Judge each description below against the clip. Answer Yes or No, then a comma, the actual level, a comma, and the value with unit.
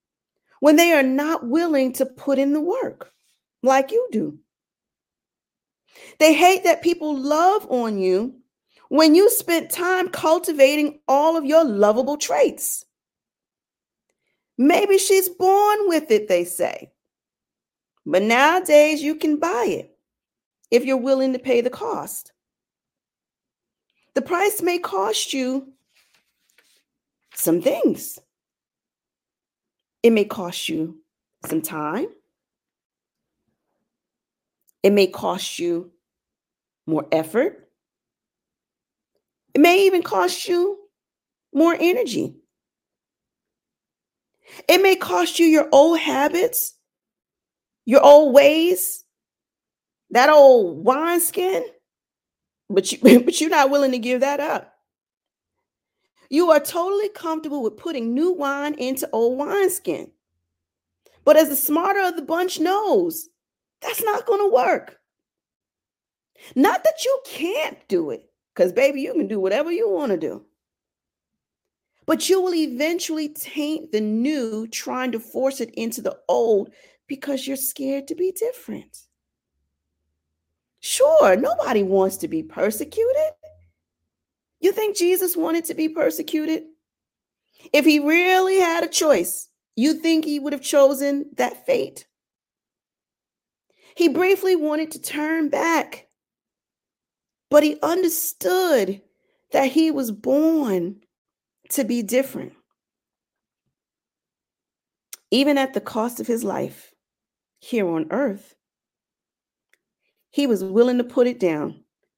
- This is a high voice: Yes, very high, 300 Hz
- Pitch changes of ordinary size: No, wide, 5.7 semitones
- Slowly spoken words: Yes, slow, 120 wpm